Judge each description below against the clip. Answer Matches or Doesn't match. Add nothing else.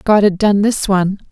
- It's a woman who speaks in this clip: Matches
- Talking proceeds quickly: Matches